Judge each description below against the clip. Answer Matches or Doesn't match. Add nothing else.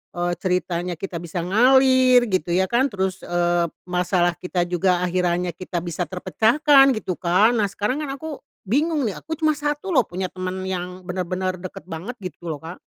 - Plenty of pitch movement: Matches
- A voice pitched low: Doesn't match